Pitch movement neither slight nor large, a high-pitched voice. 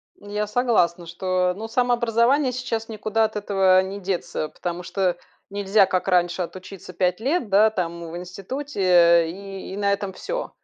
Yes: average, 3.4 semitones; high, 195 Hz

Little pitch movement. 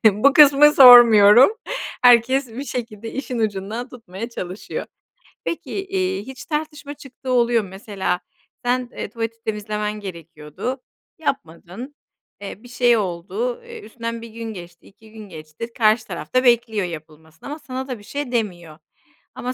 No: average, 4.3 semitones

